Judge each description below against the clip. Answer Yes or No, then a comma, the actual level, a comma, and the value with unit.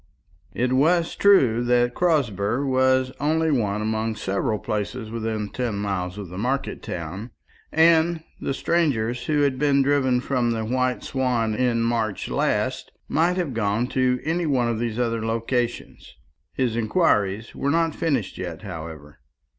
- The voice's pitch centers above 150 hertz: No, low, 120 Hz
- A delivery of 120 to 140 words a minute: No, average, 150 wpm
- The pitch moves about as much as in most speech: Yes, average, 4.2 semitones